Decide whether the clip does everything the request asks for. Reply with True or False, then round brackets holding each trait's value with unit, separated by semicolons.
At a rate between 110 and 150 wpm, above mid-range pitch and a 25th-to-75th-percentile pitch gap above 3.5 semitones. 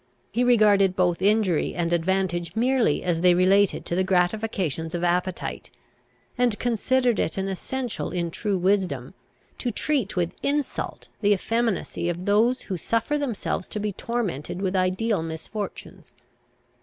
True (145 wpm; 195 Hz; 4.3 semitones)